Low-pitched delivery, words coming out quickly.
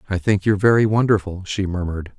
No: low, 100 Hz; average, 190 wpm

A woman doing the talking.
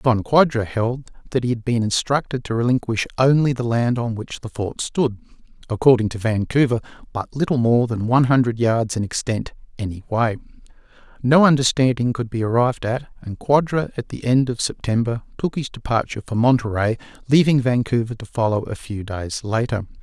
No: male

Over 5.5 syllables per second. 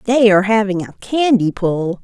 No: 4.8 syllables/s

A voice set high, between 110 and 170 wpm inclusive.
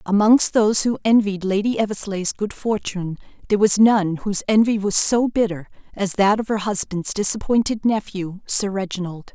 Yes: high, 205 Hz; average, 160 wpm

